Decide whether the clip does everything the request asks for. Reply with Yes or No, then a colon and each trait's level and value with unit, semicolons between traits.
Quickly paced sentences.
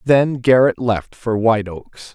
No: average, 170 wpm